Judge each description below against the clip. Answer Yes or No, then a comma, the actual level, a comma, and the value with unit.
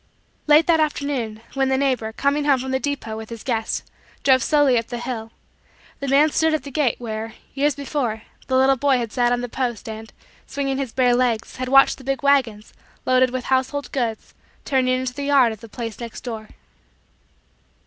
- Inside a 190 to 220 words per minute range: Yes, average, 195 wpm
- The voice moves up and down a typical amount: Yes, average, 3.3 semitones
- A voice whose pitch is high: Yes, very high, 255 Hz